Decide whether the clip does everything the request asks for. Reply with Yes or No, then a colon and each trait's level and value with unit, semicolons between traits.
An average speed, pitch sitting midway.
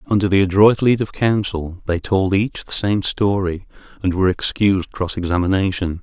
No: average, 170 wpm; very low, 95 Hz